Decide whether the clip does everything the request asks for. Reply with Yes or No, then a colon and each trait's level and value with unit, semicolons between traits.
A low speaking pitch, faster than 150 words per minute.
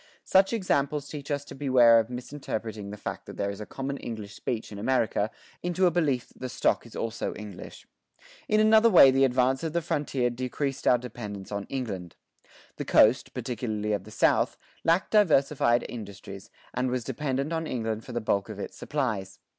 Yes: low, 125 Hz; average, 190 wpm